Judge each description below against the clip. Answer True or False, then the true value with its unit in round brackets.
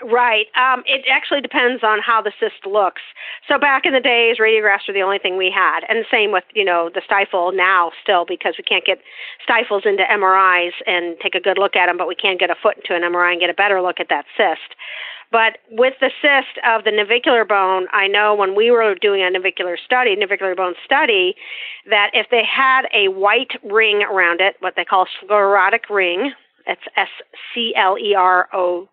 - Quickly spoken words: True (215 wpm)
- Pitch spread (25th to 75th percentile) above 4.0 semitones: True (4.5 semitones)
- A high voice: True (205 Hz)